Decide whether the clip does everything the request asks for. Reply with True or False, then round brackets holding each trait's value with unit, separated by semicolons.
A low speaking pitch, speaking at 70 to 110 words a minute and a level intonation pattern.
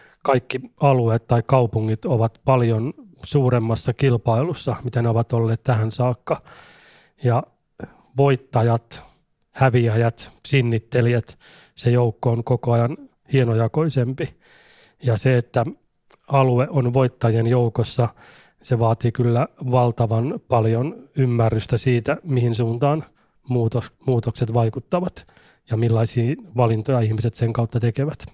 True (120 Hz; 105 wpm; 2.1 semitones)